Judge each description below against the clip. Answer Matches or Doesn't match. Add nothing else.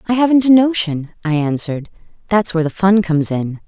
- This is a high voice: Doesn't match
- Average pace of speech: Matches